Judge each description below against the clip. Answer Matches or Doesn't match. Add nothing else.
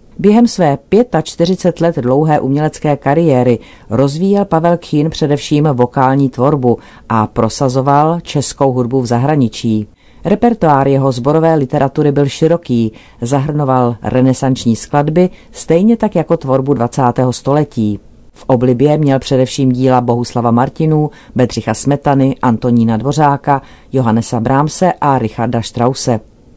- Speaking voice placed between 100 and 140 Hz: Matches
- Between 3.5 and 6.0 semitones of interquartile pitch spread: Matches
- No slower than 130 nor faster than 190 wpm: Doesn't match